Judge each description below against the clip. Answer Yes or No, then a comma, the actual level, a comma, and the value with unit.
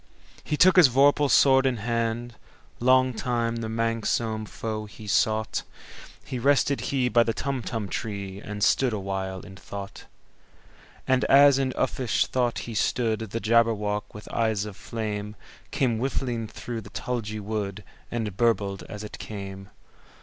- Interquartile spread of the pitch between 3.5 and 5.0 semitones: No, average, 3.0 semitones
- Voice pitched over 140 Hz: No, low, 115 Hz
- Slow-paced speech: Yes, slow, 130 wpm